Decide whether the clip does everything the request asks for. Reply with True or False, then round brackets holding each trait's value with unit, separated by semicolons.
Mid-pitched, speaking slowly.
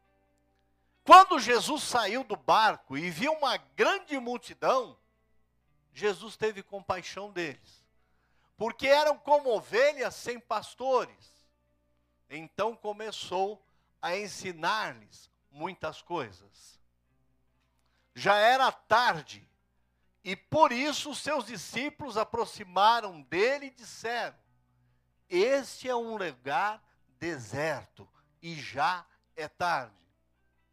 True (180 Hz; 90 wpm)